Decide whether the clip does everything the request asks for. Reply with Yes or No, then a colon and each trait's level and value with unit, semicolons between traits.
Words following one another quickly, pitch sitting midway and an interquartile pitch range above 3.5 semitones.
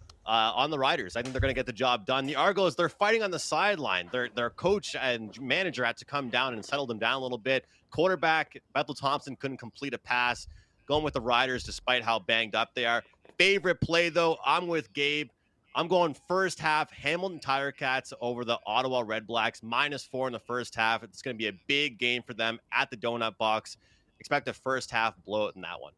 No: fast, 225 wpm; low, 125 Hz; average, 3.9 semitones